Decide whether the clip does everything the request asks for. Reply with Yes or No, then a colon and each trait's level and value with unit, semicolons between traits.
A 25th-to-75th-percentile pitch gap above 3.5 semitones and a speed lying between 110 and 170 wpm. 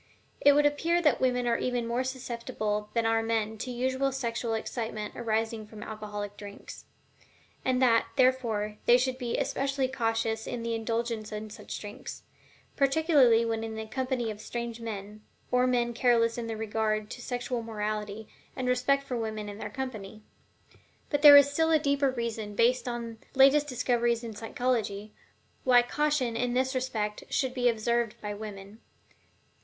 No: average, 2.8 semitones; average, 165 wpm